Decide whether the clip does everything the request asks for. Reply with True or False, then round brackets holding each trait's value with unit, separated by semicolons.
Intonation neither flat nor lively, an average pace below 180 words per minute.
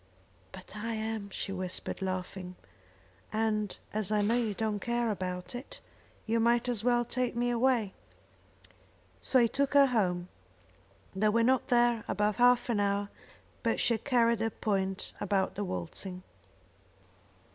True (3.5 semitones; 150 wpm)